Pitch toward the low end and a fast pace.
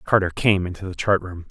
Yes: very low, 95 Hz; fast, 240 wpm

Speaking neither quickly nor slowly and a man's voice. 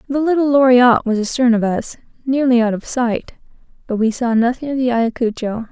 No: average, 190 wpm; female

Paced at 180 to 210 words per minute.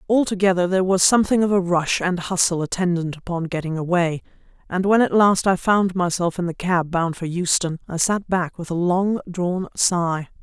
Yes: average, 195 wpm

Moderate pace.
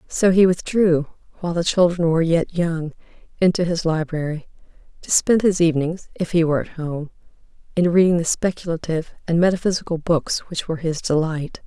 Yes: average, 165 wpm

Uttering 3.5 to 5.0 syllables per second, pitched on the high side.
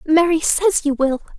Yes: 4.5 syllables/s; very high, 315 Hz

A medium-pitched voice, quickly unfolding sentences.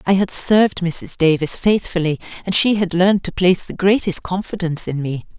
No: medium, 180 Hz; average, 190 wpm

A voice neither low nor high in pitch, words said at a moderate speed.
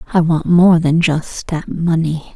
Yes: medium, 165 Hz; average, 180 wpm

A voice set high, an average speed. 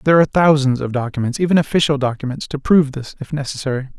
No: medium, 140 Hz; average, 195 wpm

